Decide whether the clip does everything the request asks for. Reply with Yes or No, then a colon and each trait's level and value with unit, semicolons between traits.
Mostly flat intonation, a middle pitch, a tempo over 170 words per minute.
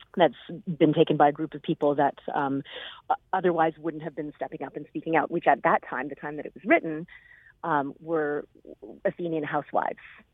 Yes: narrow, 2.1 semitones; medium, 155 Hz; average, 190 wpm